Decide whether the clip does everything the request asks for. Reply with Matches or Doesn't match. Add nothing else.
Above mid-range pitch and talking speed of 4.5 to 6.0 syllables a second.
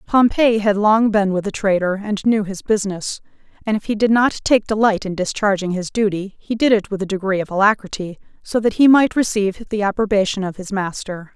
Matches